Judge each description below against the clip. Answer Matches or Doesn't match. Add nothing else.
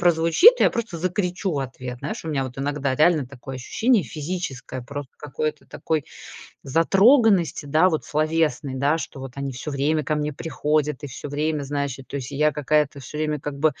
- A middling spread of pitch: Matches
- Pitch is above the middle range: Doesn't match